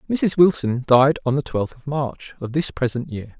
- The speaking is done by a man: Yes, male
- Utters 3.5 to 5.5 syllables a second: Yes, 4.7 syllables/s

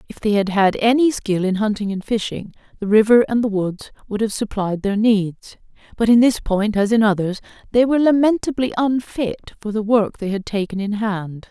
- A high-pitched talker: Yes, high, 215 Hz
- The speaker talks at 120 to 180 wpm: No, fast, 205 wpm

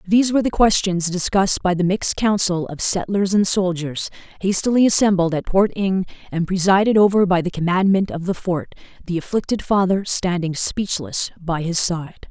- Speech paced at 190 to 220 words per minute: No, average, 165 wpm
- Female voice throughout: Yes, female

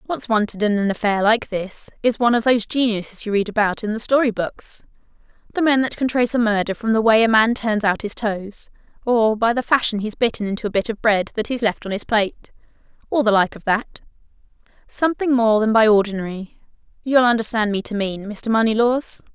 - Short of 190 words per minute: No, fast, 205 wpm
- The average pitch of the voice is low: No, high, 220 Hz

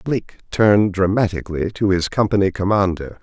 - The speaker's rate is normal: No, slow, 130 wpm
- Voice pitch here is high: No, low, 100 Hz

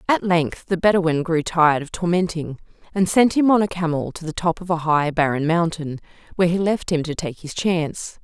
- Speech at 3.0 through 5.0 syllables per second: No, 5.3 syllables/s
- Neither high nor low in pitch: Yes, medium, 170 Hz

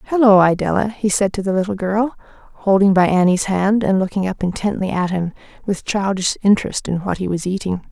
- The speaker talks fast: No, average, 195 wpm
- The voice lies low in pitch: No, high, 195 Hz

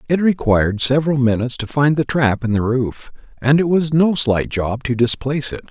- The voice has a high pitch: No, low, 135 Hz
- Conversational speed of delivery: No, fast, 210 wpm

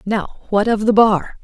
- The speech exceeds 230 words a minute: No, fast, 210 wpm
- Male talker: No, female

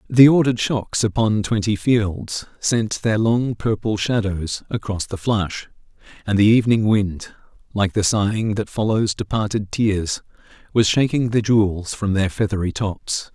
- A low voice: Yes, low, 105 Hz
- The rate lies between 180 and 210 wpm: No, average, 150 wpm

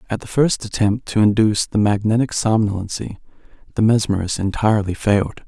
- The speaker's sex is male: Yes, male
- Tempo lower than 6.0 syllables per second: Yes, 5.8 syllables/s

